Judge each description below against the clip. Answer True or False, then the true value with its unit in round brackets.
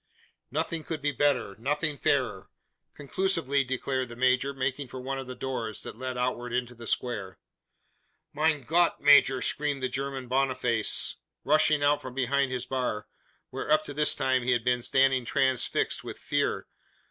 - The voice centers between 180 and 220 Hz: False (130 Hz)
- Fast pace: False (165 wpm)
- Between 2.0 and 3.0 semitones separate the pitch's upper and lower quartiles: True (2.4 semitones)